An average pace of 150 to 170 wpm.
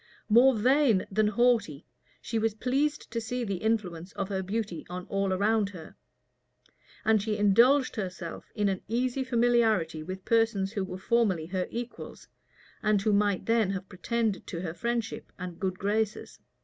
Yes: average, 160 wpm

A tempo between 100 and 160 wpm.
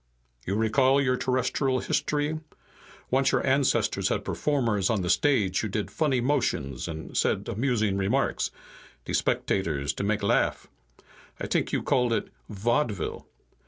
Yes: average, 140 wpm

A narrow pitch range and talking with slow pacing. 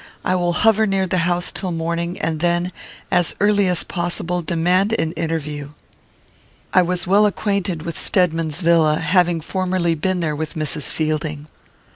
No: narrow, 2.2 semitones; average, 155 wpm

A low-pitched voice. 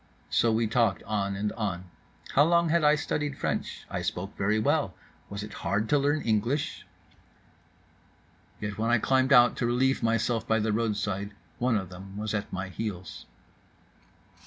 Yes: low, 110 Hz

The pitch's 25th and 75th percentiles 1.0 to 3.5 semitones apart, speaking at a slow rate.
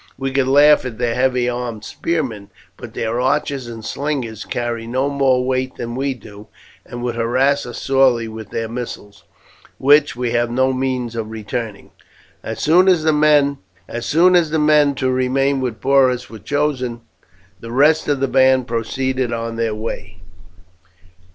No: average, 3.1 semitones; average, 155 wpm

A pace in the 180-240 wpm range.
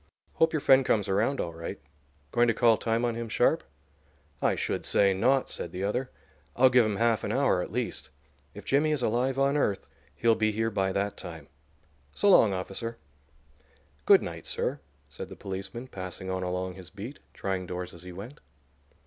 Yes: average, 190 wpm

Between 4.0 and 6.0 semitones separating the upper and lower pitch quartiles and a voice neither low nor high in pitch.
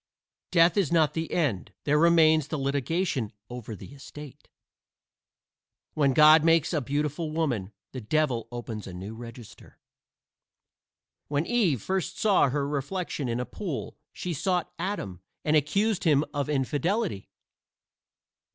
Yes: average, 4.7 semitones; medium, 150 Hz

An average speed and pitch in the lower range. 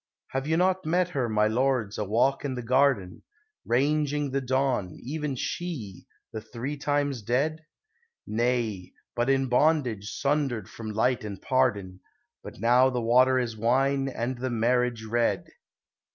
Yes: average, 150 wpm; low, 125 Hz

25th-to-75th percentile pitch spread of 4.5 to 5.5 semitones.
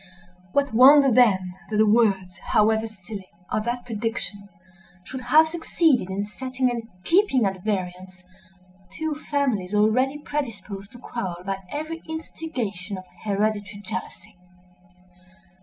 Yes: average, 5.1 semitones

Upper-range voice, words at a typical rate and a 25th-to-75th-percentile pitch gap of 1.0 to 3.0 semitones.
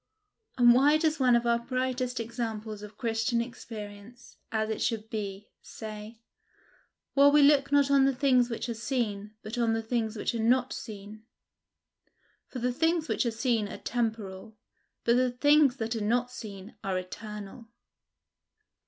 Yes: high, 235 Hz; average, 160 wpm; average, 2.7 semitones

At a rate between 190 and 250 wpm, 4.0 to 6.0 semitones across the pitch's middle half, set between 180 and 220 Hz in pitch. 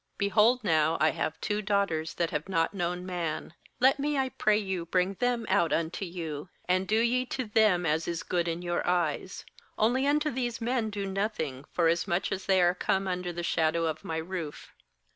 Yes: average, 195 wpm; average, 4.3 semitones; medium, 185 Hz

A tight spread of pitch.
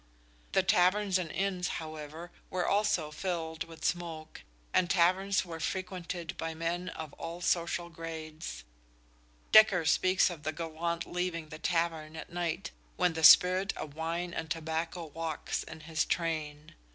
Yes: narrow, 2.0 semitones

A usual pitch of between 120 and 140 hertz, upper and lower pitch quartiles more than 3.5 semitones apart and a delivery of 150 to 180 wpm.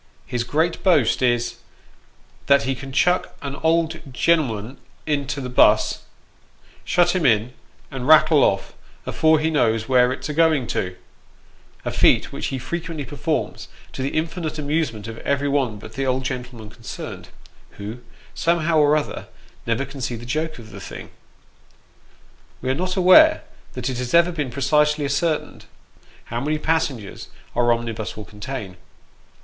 Yes: low, 135 Hz; average, 4.6 semitones; average, 160 wpm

